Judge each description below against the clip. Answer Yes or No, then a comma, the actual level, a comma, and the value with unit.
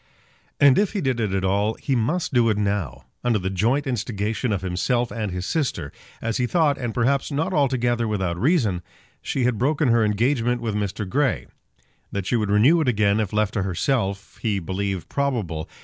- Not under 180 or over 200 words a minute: Yes, average, 195 wpm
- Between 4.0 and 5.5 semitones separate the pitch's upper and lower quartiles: Yes, average, 4.6 semitones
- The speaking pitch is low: Yes, low, 115 Hz